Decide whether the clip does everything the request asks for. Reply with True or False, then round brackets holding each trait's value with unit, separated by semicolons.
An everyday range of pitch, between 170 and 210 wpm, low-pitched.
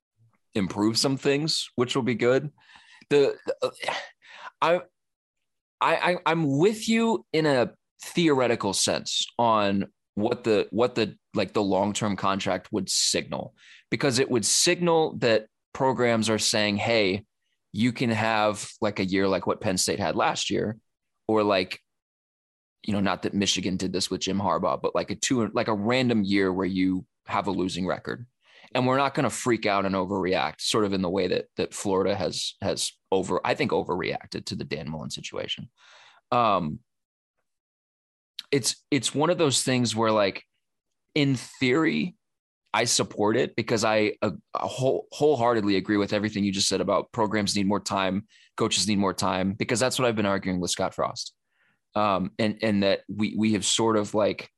True (4.5 semitones; 175 wpm; 110 Hz)